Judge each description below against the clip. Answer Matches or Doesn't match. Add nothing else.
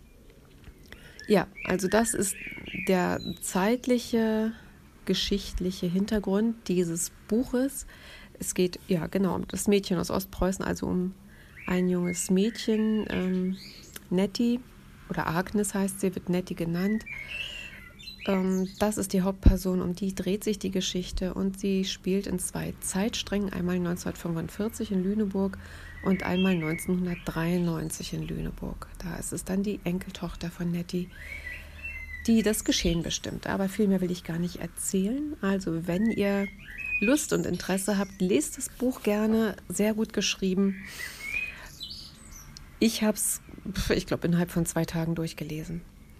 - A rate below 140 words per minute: Matches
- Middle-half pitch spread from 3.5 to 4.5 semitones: Doesn't match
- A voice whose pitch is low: Doesn't match